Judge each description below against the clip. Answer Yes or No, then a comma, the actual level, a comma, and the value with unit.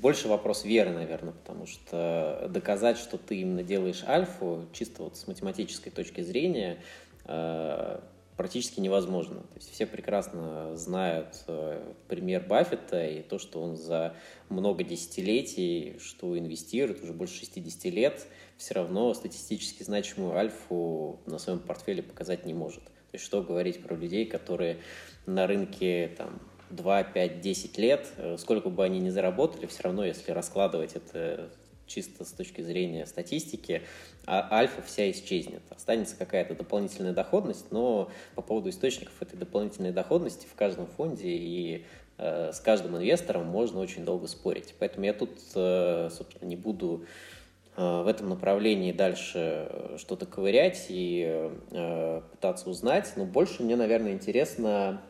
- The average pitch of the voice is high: No, very low, 90 Hz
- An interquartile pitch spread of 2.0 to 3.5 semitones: Yes, average, 2.8 semitones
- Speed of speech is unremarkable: Yes, average, 135 wpm